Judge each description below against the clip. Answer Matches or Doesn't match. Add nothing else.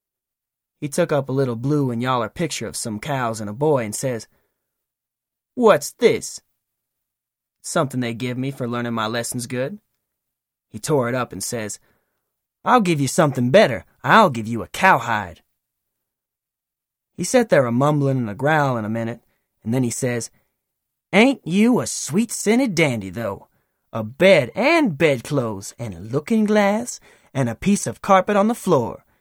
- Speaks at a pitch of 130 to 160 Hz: Matches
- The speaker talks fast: Doesn't match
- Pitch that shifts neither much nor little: Doesn't match